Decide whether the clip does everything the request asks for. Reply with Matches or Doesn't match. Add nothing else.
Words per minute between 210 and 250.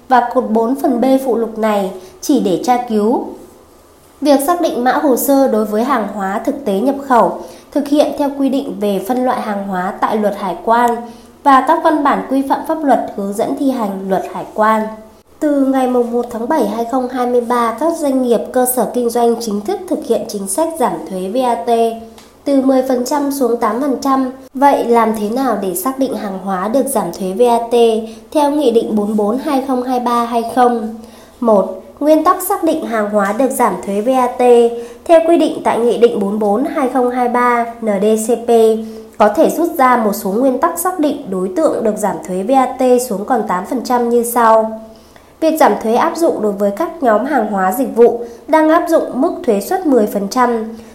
Doesn't match